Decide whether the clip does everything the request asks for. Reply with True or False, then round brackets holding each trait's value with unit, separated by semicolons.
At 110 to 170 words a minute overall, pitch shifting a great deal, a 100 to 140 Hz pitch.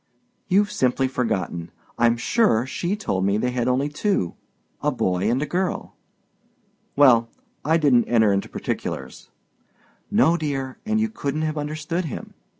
True (145 wpm; 5.7 semitones; 135 Hz)